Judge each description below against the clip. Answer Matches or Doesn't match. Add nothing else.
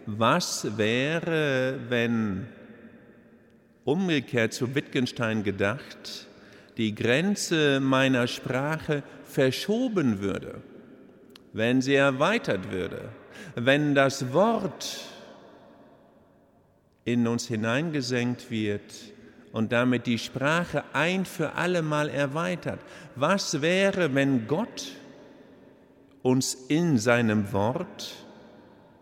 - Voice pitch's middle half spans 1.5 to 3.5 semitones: Doesn't match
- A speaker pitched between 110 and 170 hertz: Matches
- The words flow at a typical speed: Doesn't match